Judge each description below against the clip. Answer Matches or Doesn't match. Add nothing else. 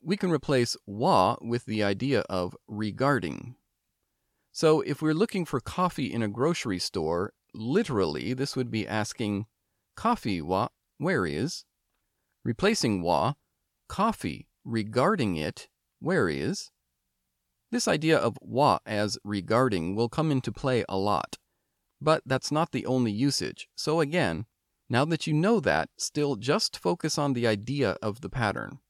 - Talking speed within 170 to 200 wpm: Doesn't match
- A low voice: Matches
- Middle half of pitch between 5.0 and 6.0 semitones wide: Matches